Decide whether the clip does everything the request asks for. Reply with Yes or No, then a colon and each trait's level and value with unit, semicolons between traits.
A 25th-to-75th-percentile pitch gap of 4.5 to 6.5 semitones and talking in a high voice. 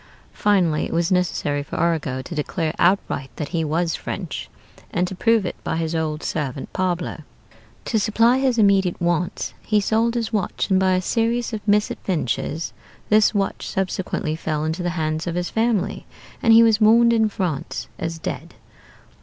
No: average, 4.9 semitones; medium, 180 Hz